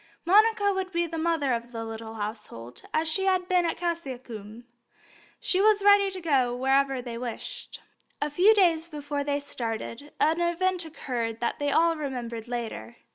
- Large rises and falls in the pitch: Yes, wide, 6.5 semitones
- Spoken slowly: No, average, 170 wpm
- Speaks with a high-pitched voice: Yes, very high, 290 Hz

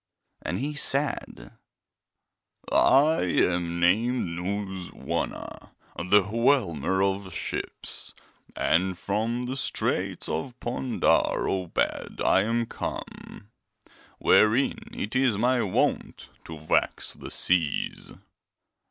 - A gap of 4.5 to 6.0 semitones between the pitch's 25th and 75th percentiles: Yes, wide, 5.6 semitones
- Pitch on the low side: Yes, low, 100 Hz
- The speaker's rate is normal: No, slow, 100 wpm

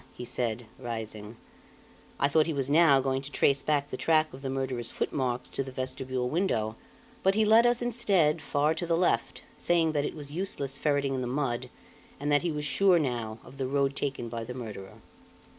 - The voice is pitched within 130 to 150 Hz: Yes, medium, 140 Hz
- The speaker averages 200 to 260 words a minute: Yes, fast, 205 wpm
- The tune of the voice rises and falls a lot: No, average, 4.0 semitones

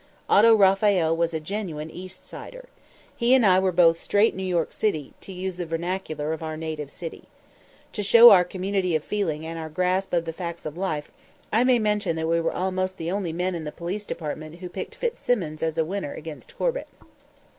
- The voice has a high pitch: No, medium, 180 Hz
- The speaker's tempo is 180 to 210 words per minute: Yes, average, 200 wpm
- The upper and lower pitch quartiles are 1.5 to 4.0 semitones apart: Yes, average, 3.5 semitones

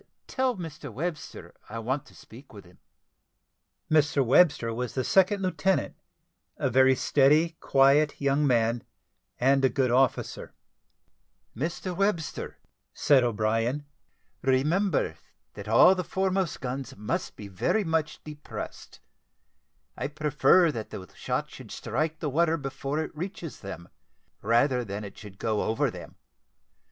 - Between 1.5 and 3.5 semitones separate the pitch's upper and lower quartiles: No, average, 5.3 semitones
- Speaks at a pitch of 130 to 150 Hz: Yes, medium, 140 Hz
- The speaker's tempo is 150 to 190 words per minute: No, slow, 135 wpm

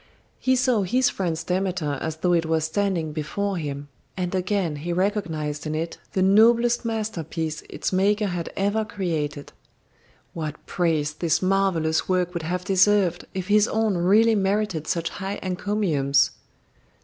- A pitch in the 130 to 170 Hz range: No, medium, 180 Hz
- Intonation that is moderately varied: Yes, average, 4.2 semitones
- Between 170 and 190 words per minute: No, average, 150 wpm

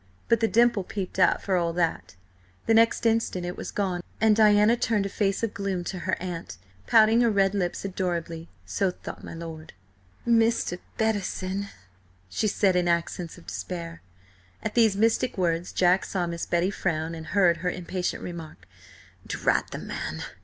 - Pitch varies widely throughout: No, average, 3.6 semitones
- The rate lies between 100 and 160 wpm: No, average, 170 wpm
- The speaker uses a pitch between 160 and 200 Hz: Yes, medium, 185 Hz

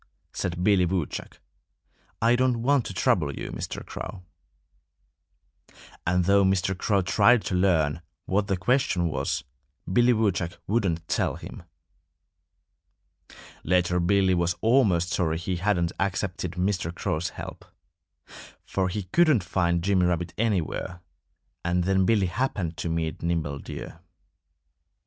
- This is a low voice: Yes, very low, 90 Hz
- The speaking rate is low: Yes, slow, 125 wpm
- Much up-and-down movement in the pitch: No, average, 2.7 semitones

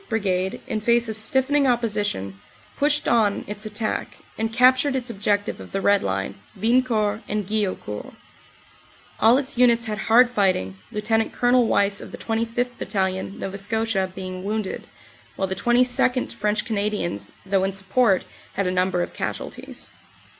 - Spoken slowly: No, average, 150 wpm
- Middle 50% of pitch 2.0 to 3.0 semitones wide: No, average, 3.6 semitones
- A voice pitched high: Yes, high, 210 Hz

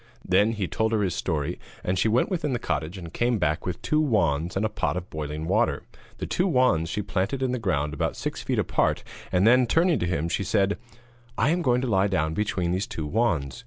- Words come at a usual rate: No, fast, 235 wpm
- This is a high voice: No, very low, 95 Hz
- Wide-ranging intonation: Yes, wide, 6.1 semitones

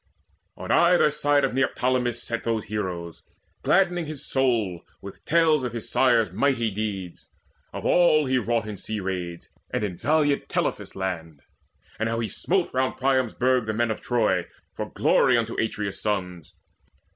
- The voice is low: Yes, low, 115 Hz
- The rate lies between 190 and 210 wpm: No, average, 160 wpm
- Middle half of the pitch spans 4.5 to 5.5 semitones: Yes, average, 4.9 semitones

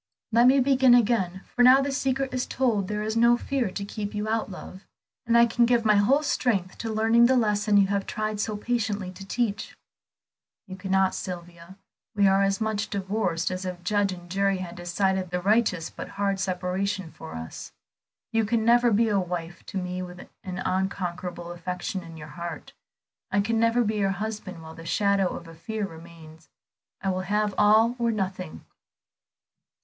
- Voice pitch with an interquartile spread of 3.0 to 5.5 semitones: Yes, average, 3.6 semitones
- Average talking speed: Yes, average, 185 wpm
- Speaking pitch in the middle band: No, high, 200 Hz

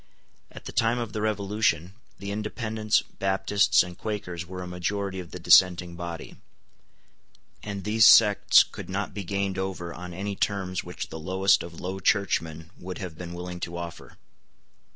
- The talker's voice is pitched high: No, very low, 95 Hz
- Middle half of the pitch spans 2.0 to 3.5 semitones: Yes, narrow, 2.6 semitones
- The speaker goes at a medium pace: Yes, average, 165 wpm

